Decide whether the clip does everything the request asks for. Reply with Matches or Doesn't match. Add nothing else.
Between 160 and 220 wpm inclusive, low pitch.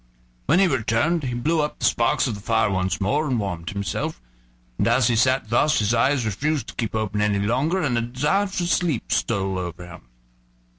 Matches